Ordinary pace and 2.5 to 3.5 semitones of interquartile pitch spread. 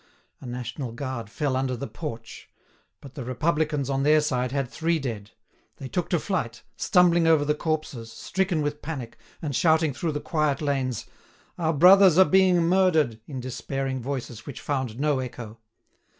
No: average, 165 wpm; average, 4.0 semitones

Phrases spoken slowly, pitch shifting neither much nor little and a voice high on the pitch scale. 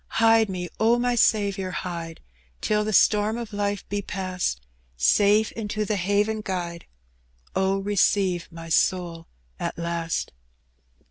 Yes: slow, 130 wpm; average, 3.1 semitones; high, 200 Hz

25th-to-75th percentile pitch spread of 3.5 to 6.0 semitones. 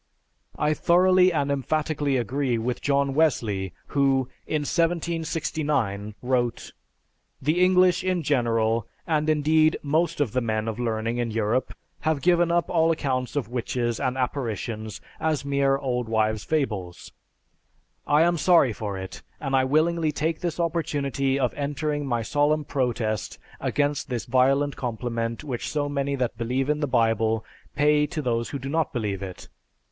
Yes: average, 4.7 semitones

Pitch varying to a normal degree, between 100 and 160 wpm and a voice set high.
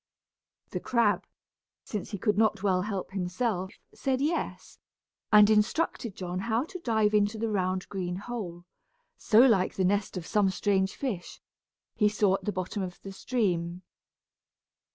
Yes: average, 3.0 semitones; average, 155 wpm; high, 205 Hz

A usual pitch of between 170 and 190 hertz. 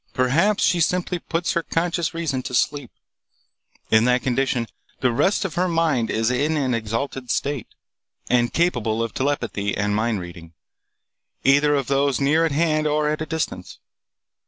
No: medium, 140 Hz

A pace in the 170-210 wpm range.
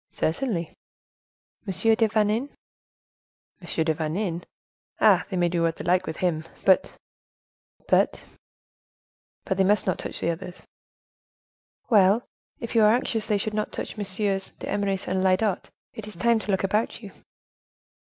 No: average, 150 wpm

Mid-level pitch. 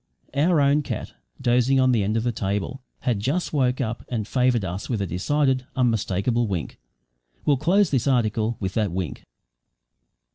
No: low, 120 Hz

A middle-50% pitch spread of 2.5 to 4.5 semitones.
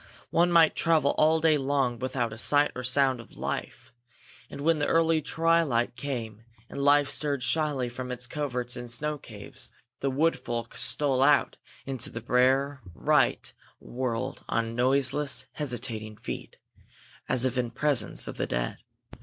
Yes: average, 3.4 semitones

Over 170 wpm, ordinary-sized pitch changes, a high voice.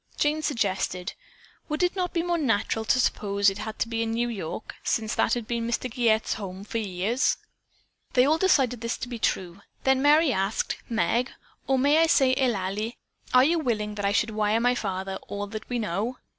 Yes: average, 200 wpm; average, 4.2 semitones; high, 230 Hz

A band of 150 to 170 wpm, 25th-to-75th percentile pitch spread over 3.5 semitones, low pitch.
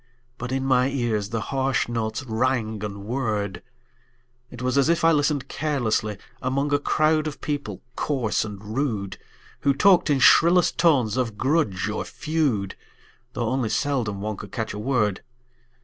Yes: average, 160 wpm; average, 4.9 semitones; low, 125 Hz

